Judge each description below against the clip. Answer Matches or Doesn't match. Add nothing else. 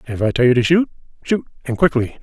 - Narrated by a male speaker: Matches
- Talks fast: Matches